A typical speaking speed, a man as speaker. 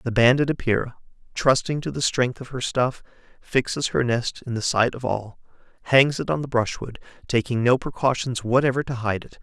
Yes: average, 190 wpm; male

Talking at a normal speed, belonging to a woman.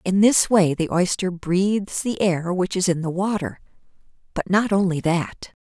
Yes: average, 180 wpm; female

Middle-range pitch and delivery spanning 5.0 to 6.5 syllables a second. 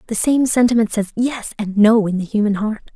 No: high, 220 Hz; 5.4 syllables/s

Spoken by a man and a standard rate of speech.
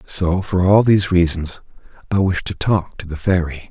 Yes: male; average, 195 wpm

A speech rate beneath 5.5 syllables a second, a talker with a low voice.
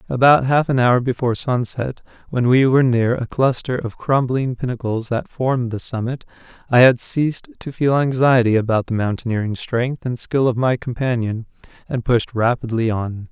Yes: 5.1 syllables/s; low, 125 Hz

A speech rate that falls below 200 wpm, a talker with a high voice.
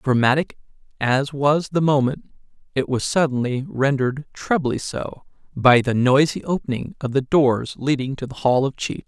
No: average, 160 wpm; low, 135 Hz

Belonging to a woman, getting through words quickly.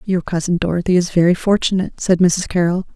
No: female; average, 185 wpm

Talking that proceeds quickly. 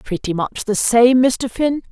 No: average, 190 wpm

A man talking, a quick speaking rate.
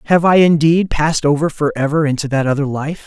No: male; average, 195 wpm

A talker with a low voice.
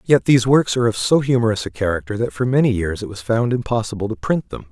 Yes: low, 115 Hz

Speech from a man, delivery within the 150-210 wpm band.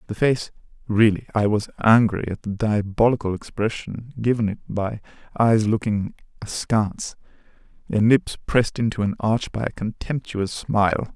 No: male; slow, 135 wpm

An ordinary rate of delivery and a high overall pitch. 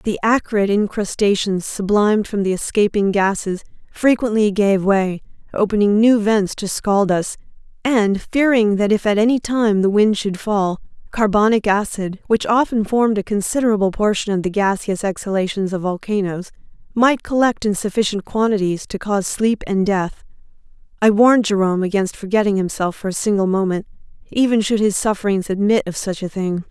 Yes: average, 160 wpm; high, 205 Hz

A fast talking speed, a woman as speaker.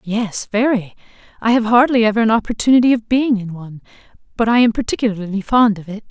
No: average, 185 wpm; female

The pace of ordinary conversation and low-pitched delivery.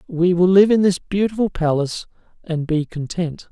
No: average, 170 wpm; medium, 175 Hz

